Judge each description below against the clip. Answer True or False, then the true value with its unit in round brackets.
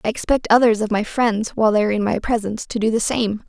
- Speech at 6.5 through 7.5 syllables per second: True (6.7 syllables/s)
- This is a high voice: True (220 Hz)